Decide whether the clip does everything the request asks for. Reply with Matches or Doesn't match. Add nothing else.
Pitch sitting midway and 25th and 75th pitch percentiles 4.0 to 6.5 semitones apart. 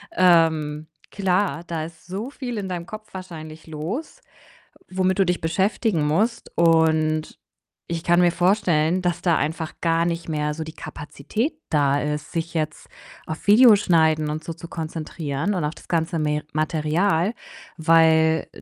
Doesn't match